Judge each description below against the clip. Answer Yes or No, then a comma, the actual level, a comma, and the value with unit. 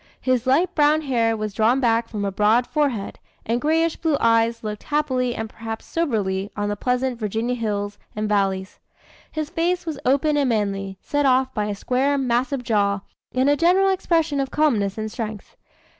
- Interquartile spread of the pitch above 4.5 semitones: Yes, average, 5.3 semitones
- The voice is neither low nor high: No, high, 240 Hz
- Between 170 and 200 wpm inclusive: Yes, average, 180 wpm